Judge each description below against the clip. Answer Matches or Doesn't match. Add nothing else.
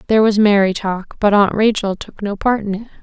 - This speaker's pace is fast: Matches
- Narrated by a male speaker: Doesn't match